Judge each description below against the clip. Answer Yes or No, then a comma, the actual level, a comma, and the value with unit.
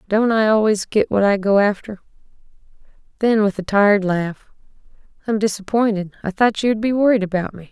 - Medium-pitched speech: No, high, 205 Hz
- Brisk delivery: No, average, 180 wpm